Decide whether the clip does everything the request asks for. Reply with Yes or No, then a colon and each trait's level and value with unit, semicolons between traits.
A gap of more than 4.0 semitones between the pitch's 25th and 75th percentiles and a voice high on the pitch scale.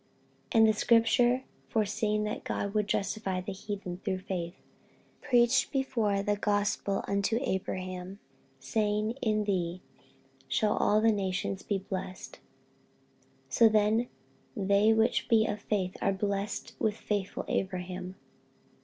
No: narrow, 2.4 semitones; high, 205 Hz